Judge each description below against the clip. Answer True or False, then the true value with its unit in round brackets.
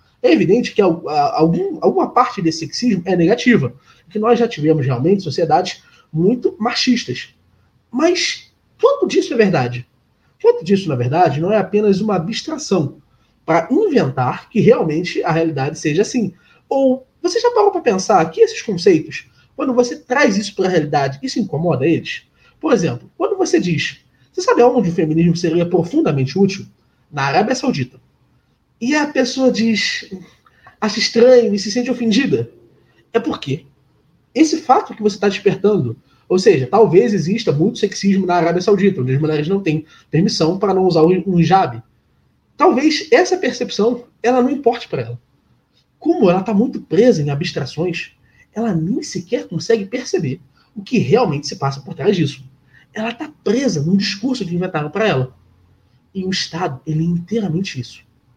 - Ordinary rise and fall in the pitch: False (7.4 semitones)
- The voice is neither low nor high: False (200 Hz)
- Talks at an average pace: True (160 wpm)